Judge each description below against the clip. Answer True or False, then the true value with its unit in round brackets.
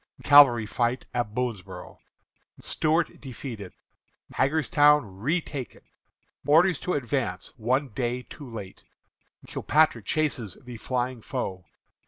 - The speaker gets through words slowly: True (100 wpm)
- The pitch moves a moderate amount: True (4.1 semitones)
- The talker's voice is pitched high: False (125 Hz)